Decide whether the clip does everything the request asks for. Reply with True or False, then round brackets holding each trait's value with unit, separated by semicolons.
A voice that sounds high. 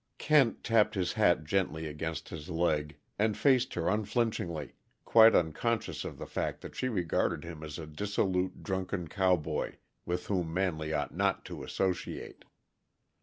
False (90 Hz)